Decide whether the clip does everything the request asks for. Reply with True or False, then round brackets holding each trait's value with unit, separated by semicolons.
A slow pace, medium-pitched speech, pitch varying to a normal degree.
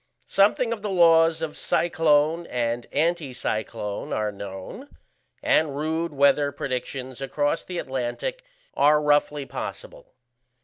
True (115 wpm; 150 Hz; 4.5 semitones)